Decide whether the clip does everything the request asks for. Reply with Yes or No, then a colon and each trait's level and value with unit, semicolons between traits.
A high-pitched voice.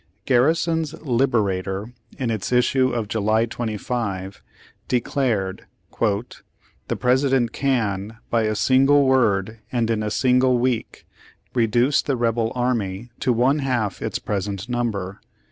No: low, 120 Hz